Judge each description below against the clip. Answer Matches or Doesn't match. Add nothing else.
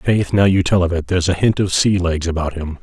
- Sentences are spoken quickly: Matches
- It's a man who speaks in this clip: Matches